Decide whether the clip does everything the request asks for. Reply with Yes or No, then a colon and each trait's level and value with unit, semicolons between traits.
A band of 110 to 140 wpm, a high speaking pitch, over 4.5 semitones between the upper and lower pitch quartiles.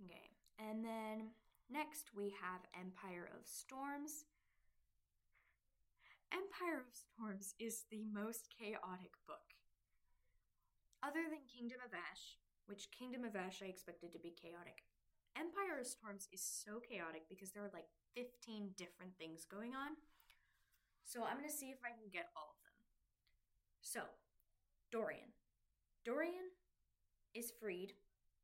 Yes: slow, 135 wpm; high, 220 Hz; average, 5.2 semitones